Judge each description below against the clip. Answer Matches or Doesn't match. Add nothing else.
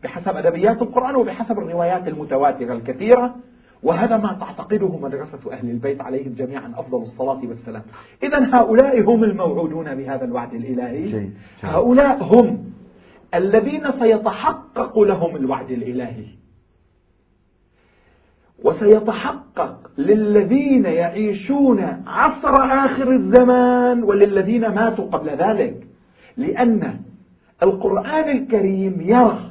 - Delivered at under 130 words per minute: Matches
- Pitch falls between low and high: Doesn't match